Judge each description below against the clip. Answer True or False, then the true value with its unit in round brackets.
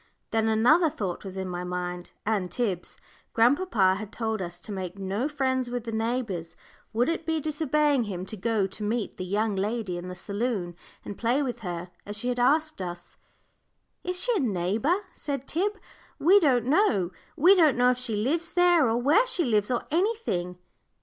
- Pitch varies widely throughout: True (7.3 semitones)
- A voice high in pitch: True (230 Hz)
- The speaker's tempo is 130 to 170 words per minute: False (190 wpm)